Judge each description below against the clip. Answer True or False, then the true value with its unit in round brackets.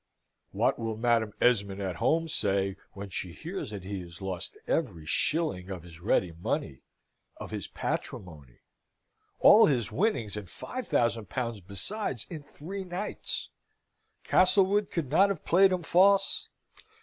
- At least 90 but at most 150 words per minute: True (145 wpm)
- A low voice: True (115 Hz)